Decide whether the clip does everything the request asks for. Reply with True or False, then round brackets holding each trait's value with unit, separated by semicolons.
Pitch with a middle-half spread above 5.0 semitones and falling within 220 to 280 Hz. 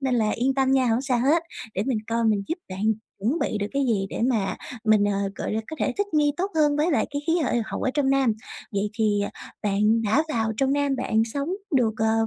False (4.4 semitones; 240 Hz)